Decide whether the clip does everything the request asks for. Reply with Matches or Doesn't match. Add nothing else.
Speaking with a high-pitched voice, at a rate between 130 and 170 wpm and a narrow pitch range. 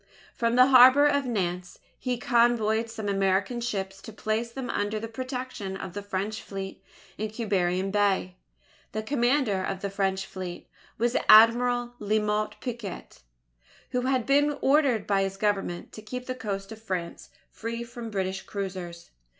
Doesn't match